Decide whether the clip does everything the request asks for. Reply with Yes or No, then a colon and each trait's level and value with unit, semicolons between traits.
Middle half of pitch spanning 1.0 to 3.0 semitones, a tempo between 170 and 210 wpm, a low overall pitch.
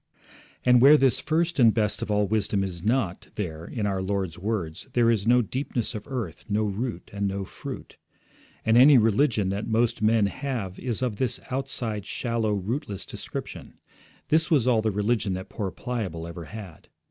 No: average, 3.9 semitones; average, 180 wpm; low, 110 Hz